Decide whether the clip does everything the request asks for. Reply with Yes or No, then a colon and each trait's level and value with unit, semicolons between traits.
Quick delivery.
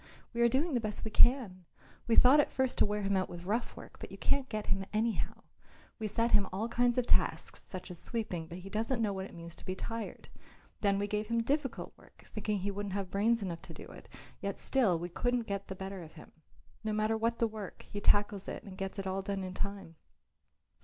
Yes: fast, 240 wpm